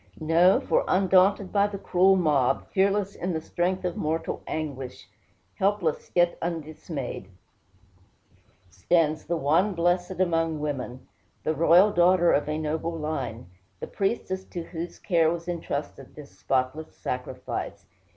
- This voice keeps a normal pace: No, slow, 130 wpm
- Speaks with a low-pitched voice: No, medium, 165 Hz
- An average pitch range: Yes, average, 3.4 semitones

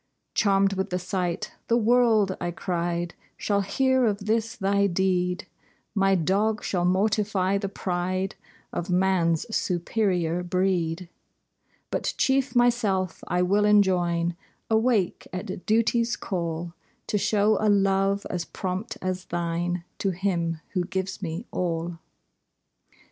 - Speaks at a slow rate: Yes, slow, 125 wpm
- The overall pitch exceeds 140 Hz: Yes, high, 190 Hz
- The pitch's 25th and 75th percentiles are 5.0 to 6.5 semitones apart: No, average, 2.8 semitones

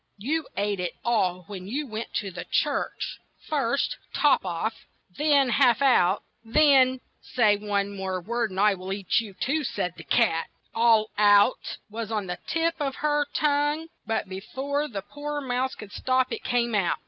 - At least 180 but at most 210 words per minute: Yes, average, 185 wpm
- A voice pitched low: No, high, 230 Hz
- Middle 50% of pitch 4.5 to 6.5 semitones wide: Yes, wide, 5.6 semitones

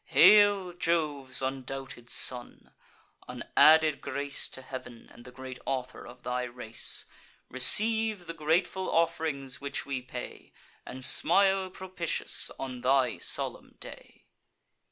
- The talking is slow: Yes, slow, 120 wpm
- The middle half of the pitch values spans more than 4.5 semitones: Yes, average, 5.0 semitones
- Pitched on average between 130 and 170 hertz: Yes, medium, 140 Hz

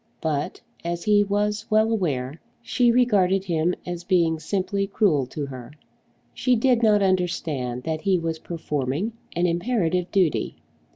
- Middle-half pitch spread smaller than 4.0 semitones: No, average, 4.5 semitones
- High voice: No, medium, 180 Hz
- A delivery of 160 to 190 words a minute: No, average, 140 wpm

